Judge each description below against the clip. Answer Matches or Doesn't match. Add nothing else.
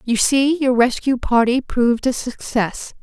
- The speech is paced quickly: Doesn't match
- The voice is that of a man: Doesn't match